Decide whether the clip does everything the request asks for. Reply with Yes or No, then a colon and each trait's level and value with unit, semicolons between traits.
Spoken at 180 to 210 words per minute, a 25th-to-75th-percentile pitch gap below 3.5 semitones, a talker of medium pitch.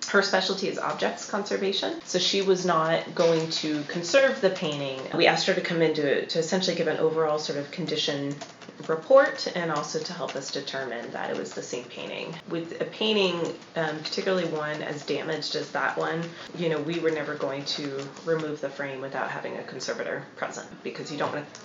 Yes: average, 200 wpm; narrow, 2.5 semitones; medium, 160 Hz